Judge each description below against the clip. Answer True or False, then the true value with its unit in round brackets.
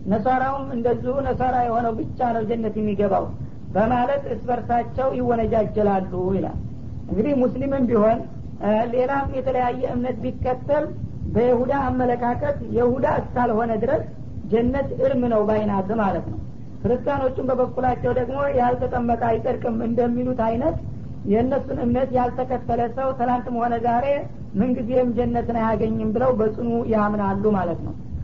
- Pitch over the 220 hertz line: True (240 Hz)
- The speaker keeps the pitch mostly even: True (2.1 semitones)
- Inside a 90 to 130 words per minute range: True (110 wpm)